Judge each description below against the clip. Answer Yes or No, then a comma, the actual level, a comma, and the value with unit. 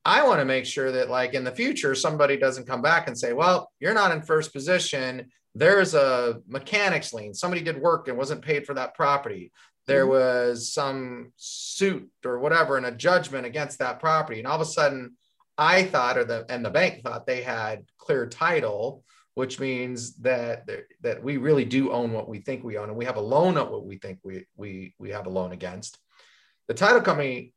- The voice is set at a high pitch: No, low, 135 Hz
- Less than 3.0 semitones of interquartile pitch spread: No, average, 4.8 semitones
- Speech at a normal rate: No, fast, 210 wpm